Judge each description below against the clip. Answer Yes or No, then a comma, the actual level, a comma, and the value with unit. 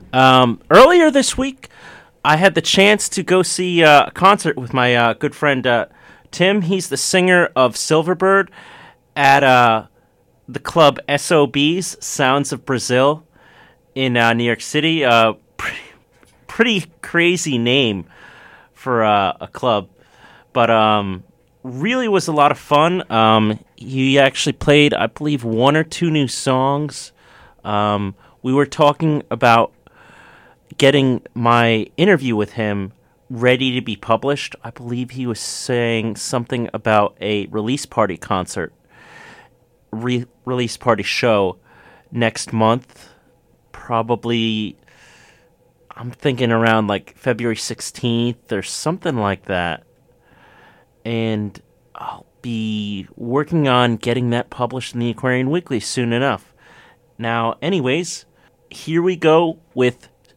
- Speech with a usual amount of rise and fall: Yes, average, 4.7 semitones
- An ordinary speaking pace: No, slow, 130 wpm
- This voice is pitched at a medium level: No, low, 125 Hz